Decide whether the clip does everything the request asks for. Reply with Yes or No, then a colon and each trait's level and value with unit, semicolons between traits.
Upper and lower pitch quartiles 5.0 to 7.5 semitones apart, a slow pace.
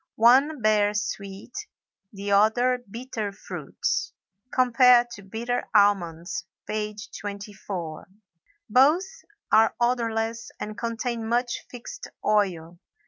No: average, 3.1 semitones; slow, 90 wpm